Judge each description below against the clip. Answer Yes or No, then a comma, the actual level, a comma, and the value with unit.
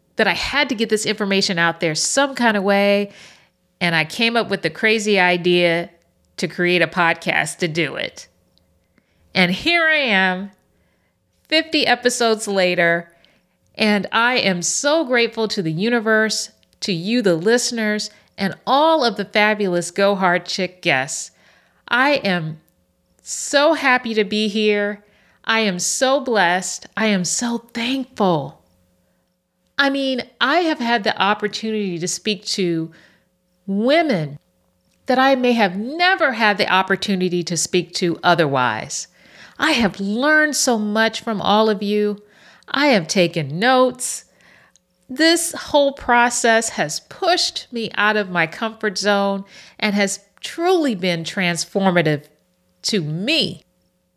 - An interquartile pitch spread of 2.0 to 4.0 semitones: No, average, 5.3 semitones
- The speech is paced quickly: No, average, 140 wpm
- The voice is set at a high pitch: Yes, high, 205 Hz